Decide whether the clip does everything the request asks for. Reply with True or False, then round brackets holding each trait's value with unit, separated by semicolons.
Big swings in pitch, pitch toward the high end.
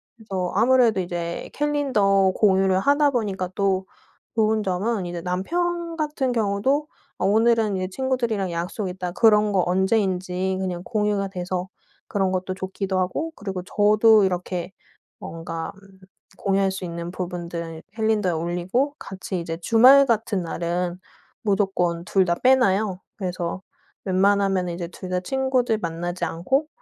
False (3.6 semitones; 195 Hz)